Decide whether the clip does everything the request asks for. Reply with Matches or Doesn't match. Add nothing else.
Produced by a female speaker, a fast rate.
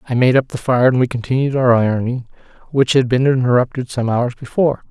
Doesn't match